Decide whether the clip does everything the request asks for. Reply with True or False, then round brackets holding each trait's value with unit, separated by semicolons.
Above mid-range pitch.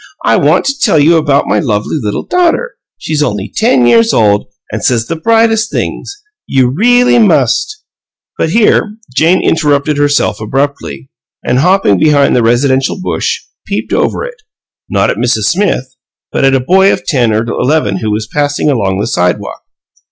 False (145 Hz)